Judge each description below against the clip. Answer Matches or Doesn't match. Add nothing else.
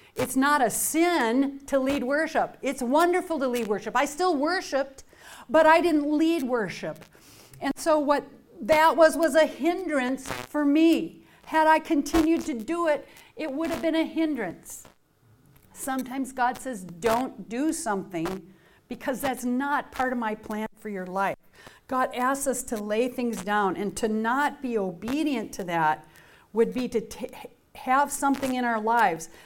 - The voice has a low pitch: Doesn't match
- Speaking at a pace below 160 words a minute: Doesn't match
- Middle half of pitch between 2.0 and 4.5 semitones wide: Doesn't match